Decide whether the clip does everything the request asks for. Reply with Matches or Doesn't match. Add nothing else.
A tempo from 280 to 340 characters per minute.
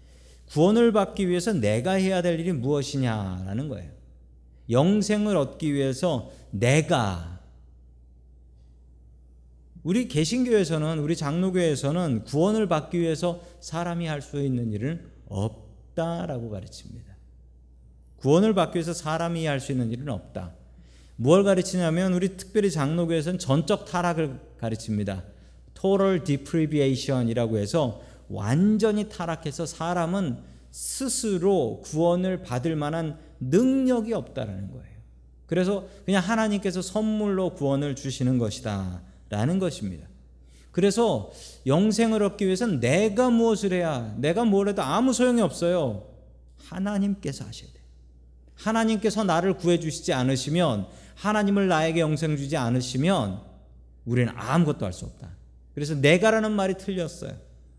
Matches